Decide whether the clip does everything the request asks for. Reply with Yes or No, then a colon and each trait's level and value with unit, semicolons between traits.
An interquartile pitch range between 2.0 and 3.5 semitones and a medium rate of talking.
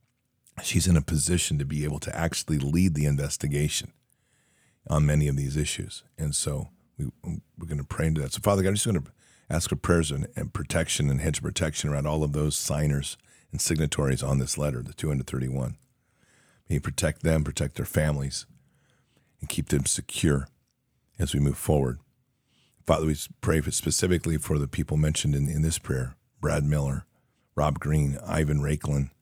Yes: average, 2.8 semitones; average, 185 wpm